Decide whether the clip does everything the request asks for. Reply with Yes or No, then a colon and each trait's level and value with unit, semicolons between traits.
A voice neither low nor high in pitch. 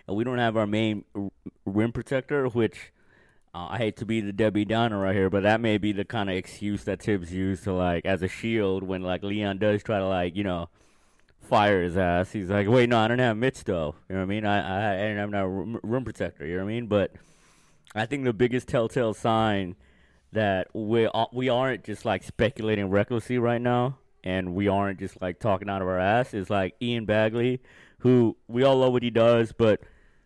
No: low, 105 Hz